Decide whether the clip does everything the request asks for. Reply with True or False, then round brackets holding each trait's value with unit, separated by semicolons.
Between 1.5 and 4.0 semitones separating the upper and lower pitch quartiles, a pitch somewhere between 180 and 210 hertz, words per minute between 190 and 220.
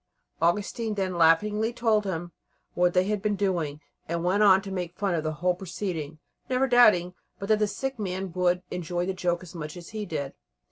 True (3.2 semitones; 185 Hz; 200 wpm)